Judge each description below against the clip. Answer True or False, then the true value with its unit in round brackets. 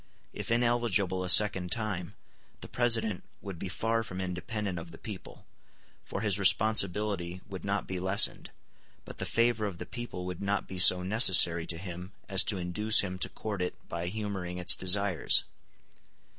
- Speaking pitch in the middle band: False (95 Hz)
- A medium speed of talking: True (170 wpm)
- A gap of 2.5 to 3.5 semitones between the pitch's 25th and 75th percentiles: True (2.9 semitones)